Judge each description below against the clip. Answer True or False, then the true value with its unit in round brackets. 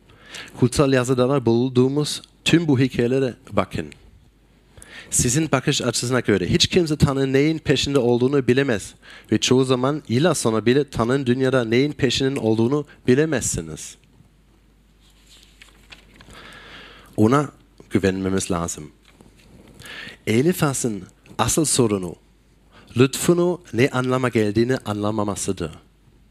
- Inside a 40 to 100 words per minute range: True (95 wpm)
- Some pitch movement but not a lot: True (4.3 semitones)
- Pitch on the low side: True (125 Hz)